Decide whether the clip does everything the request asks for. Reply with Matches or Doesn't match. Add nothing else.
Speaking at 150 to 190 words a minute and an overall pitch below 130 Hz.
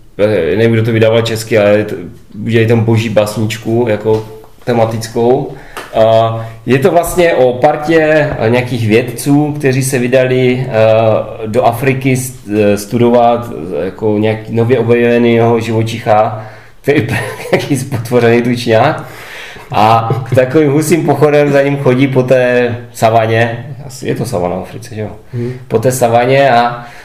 Doesn't match